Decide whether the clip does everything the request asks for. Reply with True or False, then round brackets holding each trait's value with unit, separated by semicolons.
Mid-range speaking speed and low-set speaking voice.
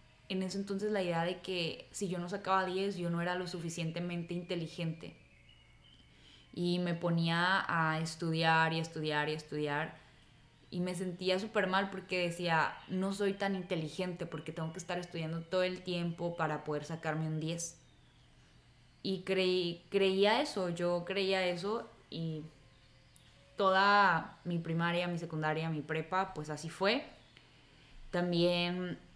False (150 wpm; 175 Hz)